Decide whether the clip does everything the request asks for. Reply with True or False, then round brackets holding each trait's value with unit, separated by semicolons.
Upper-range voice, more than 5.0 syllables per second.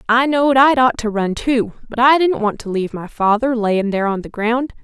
True (235 Hz; 5.5 syllables/s)